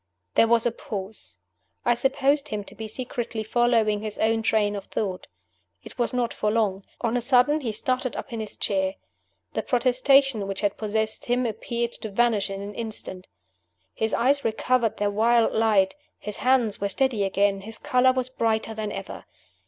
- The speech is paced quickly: No, average, 180 wpm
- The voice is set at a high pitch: Yes, high, 225 Hz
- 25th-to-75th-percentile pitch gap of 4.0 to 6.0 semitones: No, average, 3.0 semitones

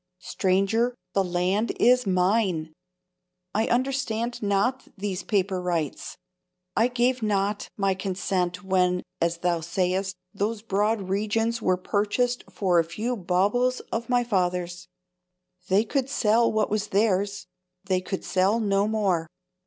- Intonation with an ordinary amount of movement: Yes, average, 3.7 semitones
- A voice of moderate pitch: No, high, 200 Hz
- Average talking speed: No, slow, 130 wpm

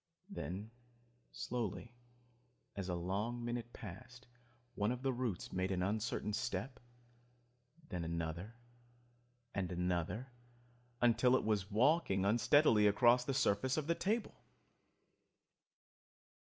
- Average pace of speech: No, slow, 110 wpm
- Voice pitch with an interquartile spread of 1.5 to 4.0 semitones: No, average, 4.7 semitones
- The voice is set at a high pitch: No, low, 110 Hz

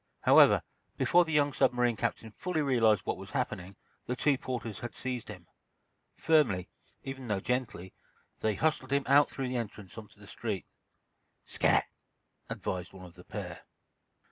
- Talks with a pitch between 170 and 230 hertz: No, low, 120 Hz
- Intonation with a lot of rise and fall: No, average, 4.7 semitones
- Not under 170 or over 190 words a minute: No, average, 155 wpm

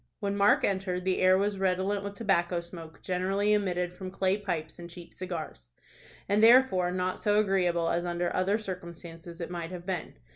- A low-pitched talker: No, medium, 185 Hz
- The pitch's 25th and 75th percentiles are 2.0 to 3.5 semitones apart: Yes, narrow, 2.4 semitones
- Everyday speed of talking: Yes, average, 180 wpm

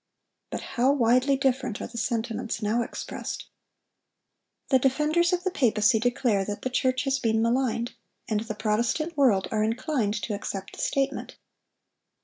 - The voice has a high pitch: Yes, high, 240 Hz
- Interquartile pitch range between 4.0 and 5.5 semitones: No, average, 3.6 semitones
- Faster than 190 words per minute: No, average, 150 wpm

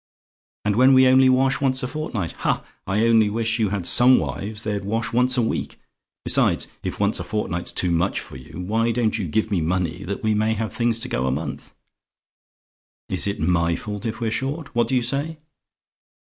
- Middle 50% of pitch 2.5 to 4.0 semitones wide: No, average, 4.4 semitones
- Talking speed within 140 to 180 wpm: No, fast, 205 wpm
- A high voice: No, low, 110 Hz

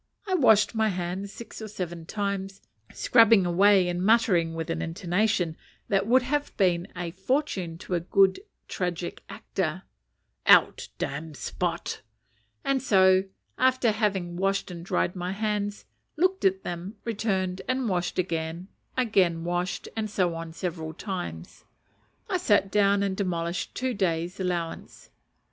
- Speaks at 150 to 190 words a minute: No, average, 140 wpm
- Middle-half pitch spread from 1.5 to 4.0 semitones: Yes, average, 3.4 semitones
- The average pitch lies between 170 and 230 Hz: Yes, high, 190 Hz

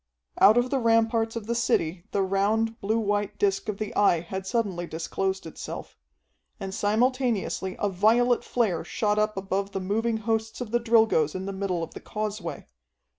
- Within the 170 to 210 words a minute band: Yes, average, 175 wpm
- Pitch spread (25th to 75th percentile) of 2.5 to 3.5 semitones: Yes, average, 2.9 semitones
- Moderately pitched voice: No, high, 210 Hz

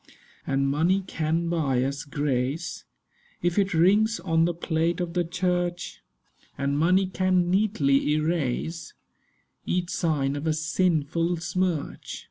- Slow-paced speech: Yes, slow, 125 wpm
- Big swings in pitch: No, average, 3.3 semitones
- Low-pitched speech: No, medium, 165 Hz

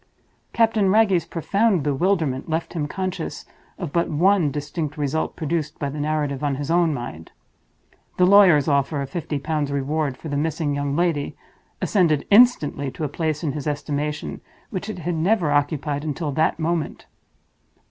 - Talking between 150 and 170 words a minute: Yes, average, 160 wpm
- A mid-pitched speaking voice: Yes, medium, 155 Hz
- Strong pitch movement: No, average, 3.3 semitones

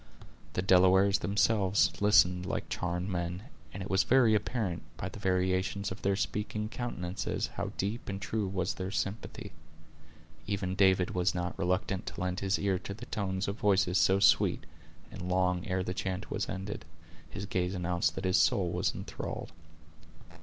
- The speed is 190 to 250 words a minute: No, average, 165 wpm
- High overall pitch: No, very low, 95 Hz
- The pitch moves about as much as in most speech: No, narrow, 1.7 semitones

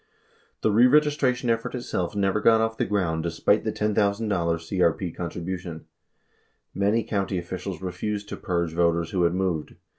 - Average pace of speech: Yes, average, 145 wpm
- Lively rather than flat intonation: No, average, 3.8 semitones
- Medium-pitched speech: No, very low, 95 Hz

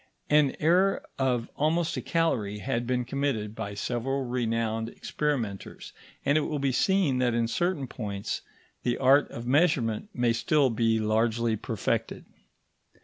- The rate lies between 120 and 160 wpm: Yes, average, 145 wpm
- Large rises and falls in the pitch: No, average, 4.1 semitones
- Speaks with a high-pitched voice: No, low, 125 Hz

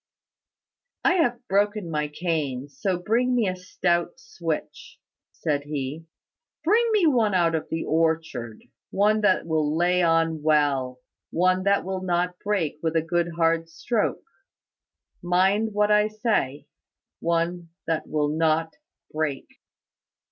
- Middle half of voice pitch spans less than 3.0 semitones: No, average, 4.2 semitones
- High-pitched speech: No, medium, 170 Hz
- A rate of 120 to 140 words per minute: Yes, slow, 135 wpm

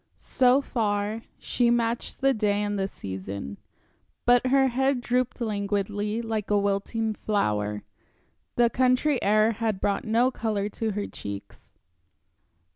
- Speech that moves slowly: Yes, slow, 130 wpm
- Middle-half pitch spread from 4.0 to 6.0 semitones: No, average, 3.1 semitones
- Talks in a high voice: Yes, high, 215 Hz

